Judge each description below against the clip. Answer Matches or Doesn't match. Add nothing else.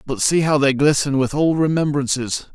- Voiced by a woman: Doesn't match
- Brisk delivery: Doesn't match